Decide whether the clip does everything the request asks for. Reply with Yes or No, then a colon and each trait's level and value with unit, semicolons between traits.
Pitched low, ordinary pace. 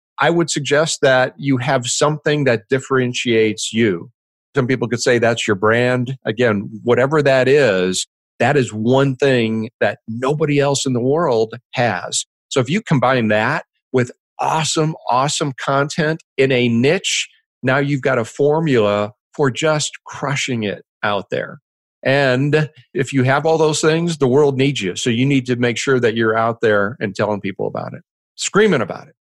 Yes: low, 130 Hz; average, 175 wpm